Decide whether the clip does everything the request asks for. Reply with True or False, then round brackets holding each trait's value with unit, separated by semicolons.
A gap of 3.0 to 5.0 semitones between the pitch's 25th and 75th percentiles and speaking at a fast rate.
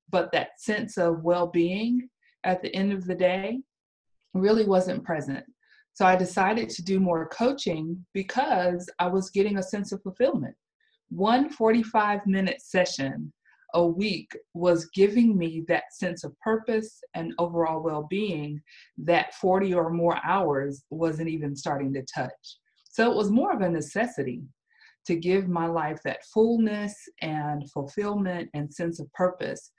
False (4.7 semitones; 155 wpm)